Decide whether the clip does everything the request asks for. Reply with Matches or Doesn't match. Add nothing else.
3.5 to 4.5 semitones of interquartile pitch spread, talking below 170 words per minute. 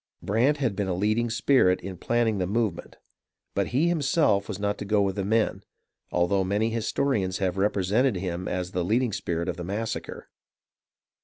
Doesn't match